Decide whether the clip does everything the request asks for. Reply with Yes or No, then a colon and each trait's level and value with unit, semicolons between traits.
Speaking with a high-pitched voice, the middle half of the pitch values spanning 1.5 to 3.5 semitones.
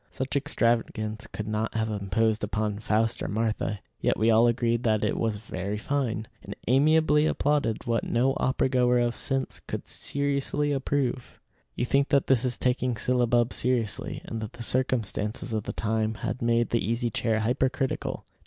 No: low, 120 Hz; average, 3.0 semitones